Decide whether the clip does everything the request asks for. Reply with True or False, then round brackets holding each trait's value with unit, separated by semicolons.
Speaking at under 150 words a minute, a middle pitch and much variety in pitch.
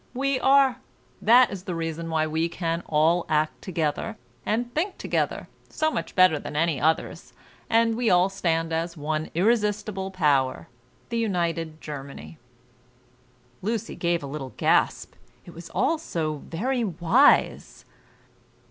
True (140 wpm; 170 Hz; 5.8 semitones)